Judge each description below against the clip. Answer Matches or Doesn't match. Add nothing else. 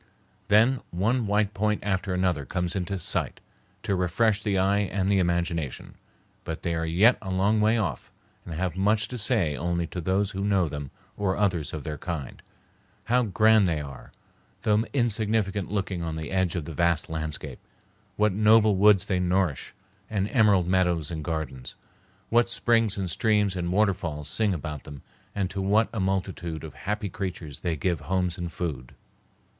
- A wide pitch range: Doesn't match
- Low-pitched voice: Matches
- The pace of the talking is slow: Doesn't match